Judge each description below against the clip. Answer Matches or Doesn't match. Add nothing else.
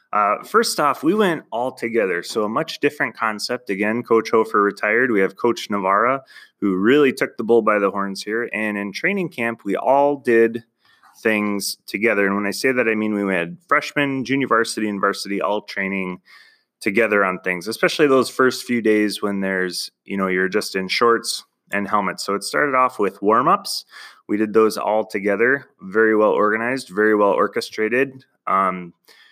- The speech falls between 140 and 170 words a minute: Doesn't match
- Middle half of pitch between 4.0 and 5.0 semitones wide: Doesn't match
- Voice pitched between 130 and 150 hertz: Doesn't match